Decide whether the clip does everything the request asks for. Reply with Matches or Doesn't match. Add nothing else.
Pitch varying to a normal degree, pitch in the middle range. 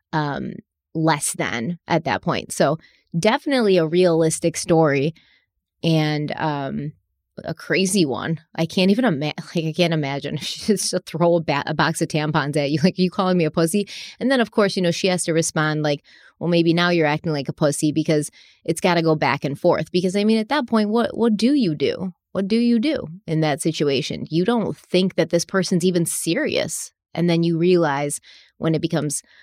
Matches